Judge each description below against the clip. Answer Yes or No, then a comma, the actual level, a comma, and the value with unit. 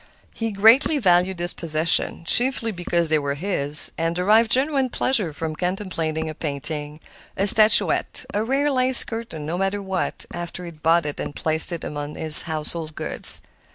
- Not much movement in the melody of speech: No, wide, 5.6 semitones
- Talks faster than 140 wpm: Yes, average, 160 wpm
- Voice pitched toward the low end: No, medium, 175 Hz